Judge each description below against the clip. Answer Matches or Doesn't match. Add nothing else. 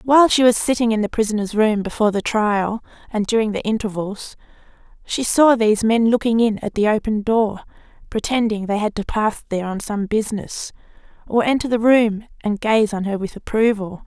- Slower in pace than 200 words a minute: Matches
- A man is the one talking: Doesn't match